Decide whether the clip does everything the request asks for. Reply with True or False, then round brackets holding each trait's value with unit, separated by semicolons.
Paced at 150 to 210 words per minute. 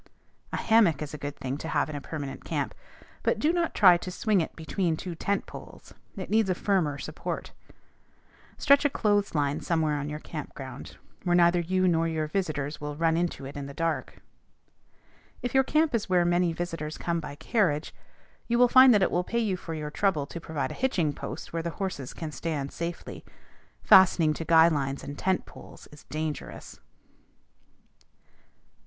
True (190 wpm)